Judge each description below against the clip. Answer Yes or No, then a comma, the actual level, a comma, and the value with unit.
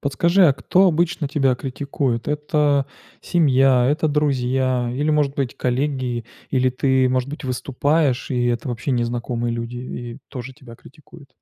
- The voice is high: No, low, 135 Hz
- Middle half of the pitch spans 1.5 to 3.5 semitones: Yes, average, 3.1 semitones